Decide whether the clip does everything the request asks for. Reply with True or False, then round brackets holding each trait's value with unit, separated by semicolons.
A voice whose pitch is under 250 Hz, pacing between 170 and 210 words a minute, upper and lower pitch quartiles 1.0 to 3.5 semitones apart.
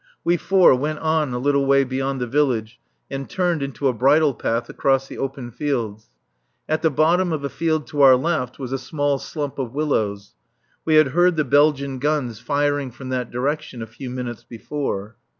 True (140 Hz; 190 wpm; 3.2 semitones)